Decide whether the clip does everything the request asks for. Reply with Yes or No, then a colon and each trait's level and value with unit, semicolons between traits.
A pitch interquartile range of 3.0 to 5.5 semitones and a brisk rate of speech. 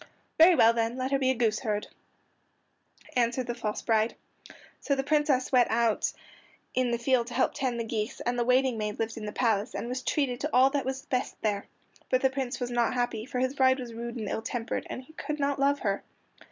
No: narrow, 2.5 semitones; fast, 230 wpm